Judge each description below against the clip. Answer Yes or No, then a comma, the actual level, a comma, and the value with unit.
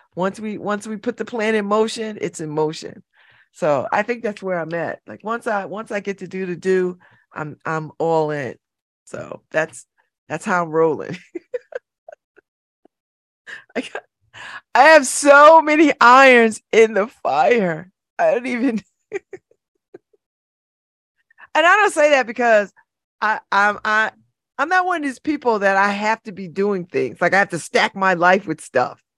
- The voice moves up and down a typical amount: No, wide, 5.9 semitones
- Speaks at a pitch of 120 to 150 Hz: No, high, 215 Hz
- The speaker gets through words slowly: No, average, 170 wpm